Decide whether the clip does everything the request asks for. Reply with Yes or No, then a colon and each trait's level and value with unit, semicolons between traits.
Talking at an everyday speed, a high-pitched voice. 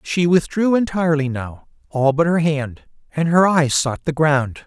No: average, 180 wpm; medium, 155 Hz